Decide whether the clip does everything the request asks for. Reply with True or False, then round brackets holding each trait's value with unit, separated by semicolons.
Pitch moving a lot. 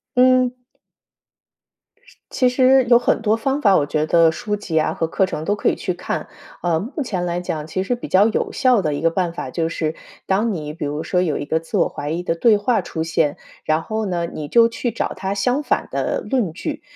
True (6.2 semitones)